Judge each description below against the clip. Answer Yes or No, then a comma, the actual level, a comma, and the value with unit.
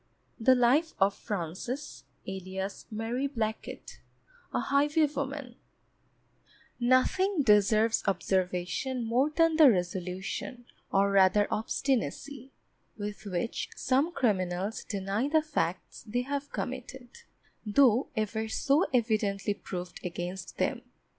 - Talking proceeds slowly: Yes, slow, 100 wpm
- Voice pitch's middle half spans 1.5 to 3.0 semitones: No, wide, 5.6 semitones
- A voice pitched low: No, high, 225 Hz